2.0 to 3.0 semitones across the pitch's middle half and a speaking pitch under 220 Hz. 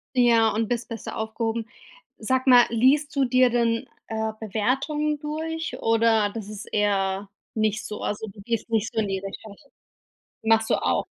No: average, 2.7 semitones; high, 225 Hz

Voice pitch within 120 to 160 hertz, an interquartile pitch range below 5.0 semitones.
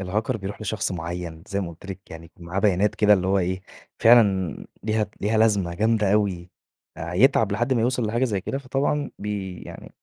No: low, 100 Hz; average, 3.4 semitones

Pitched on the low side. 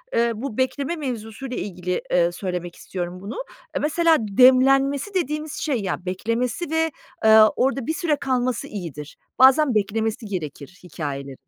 No: high, 230 Hz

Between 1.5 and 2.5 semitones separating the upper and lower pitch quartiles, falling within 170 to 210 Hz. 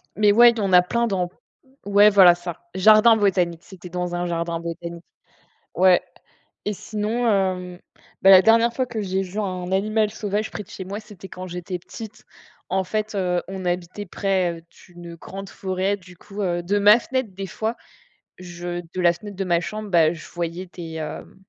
No: average, 2.9 semitones; high, 190 Hz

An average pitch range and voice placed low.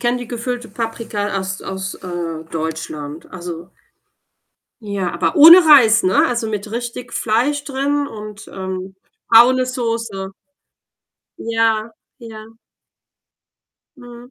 No: average, 4.2 semitones; high, 225 Hz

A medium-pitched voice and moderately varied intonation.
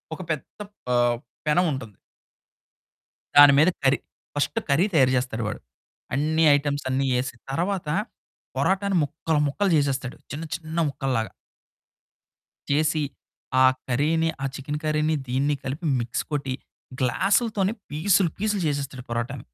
Yes: medium, 145 Hz; average, 3.7 semitones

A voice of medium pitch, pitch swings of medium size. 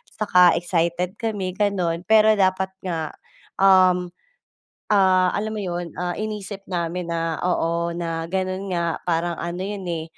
No: medium, 180 Hz; narrow, 2.2 semitones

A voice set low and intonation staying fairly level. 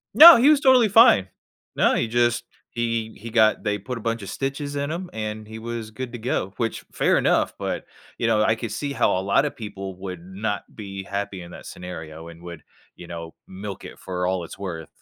No: low, 110 Hz; average, 4.1 semitones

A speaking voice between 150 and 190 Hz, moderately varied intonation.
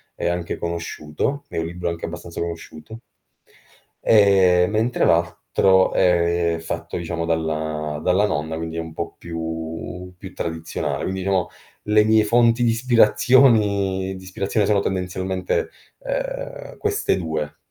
No: very low, 90 Hz; average, 4.3 semitones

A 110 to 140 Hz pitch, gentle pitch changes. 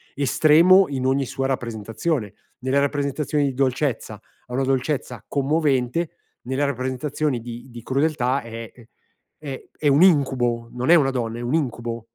No: low, 135 Hz; average, 3.2 semitones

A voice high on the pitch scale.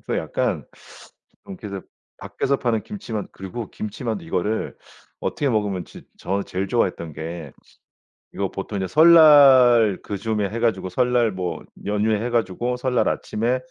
No: low, 110 Hz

